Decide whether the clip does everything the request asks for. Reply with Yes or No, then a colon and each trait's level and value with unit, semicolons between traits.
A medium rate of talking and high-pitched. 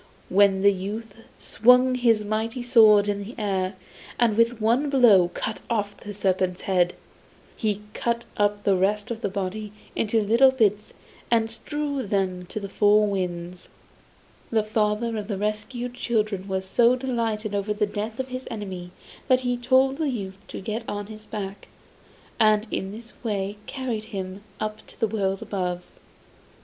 Yes: average, 165 wpm; high, 210 Hz